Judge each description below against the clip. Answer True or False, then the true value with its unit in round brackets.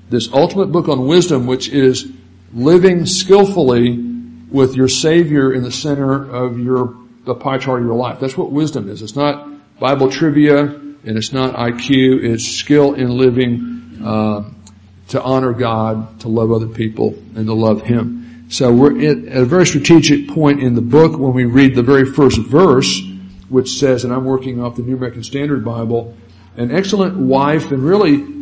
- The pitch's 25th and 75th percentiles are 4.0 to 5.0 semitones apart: False (3.4 semitones)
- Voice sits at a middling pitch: False (130 Hz)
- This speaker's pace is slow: False (175 wpm)